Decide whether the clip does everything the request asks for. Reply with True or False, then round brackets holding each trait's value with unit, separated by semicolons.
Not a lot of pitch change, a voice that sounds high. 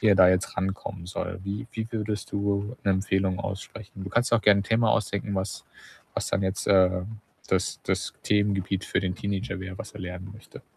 False (1.7 semitones; 100 Hz)